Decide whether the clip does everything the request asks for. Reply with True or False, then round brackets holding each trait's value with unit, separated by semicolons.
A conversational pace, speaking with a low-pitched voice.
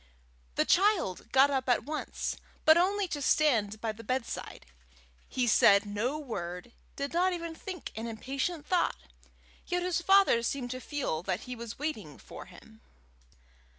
False (160 wpm; 265 Hz)